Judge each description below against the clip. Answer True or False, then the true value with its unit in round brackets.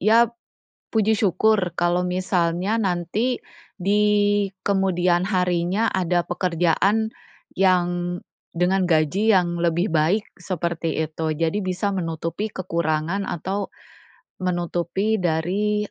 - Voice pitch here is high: False (180 Hz)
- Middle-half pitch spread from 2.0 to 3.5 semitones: True (2.9 semitones)